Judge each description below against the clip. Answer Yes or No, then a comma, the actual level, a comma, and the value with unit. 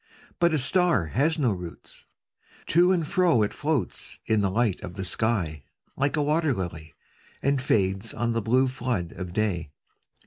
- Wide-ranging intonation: Yes, wide, 7.7 semitones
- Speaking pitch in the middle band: No, low, 115 Hz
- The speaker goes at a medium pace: Yes, average, 170 wpm